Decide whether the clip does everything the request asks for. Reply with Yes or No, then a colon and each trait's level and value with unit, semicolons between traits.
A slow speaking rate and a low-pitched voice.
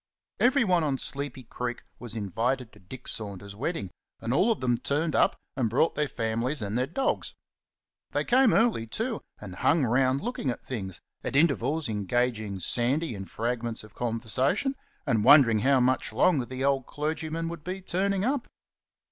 No: average, 165 wpm; low, 130 Hz